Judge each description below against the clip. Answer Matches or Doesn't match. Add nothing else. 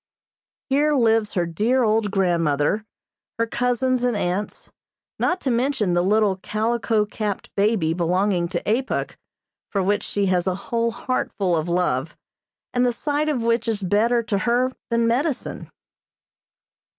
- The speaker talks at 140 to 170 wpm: Matches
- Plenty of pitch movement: Doesn't match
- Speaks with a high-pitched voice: Matches